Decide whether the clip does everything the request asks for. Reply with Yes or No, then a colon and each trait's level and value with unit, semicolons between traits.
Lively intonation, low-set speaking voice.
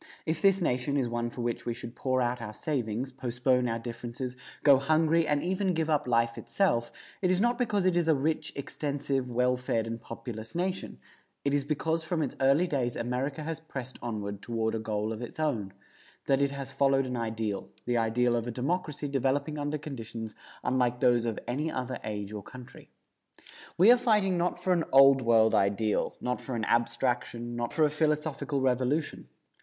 No: average, 4.4 semitones; low, 130 Hz